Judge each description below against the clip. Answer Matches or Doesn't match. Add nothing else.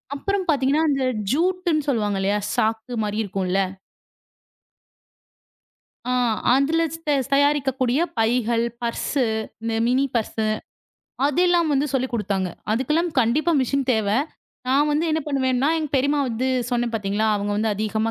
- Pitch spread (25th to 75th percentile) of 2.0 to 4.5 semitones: Doesn't match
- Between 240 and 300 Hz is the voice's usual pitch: Matches